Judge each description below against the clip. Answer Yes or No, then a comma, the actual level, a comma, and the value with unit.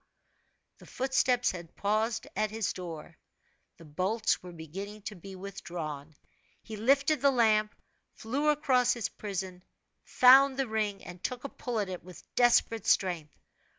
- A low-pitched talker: No, high, 210 Hz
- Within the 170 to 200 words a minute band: No, average, 150 wpm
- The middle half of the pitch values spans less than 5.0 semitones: No, average, 5.3 semitones